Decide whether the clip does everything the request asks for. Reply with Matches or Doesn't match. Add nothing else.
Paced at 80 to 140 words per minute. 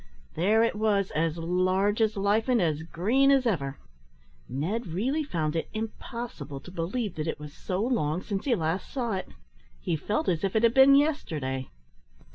Doesn't match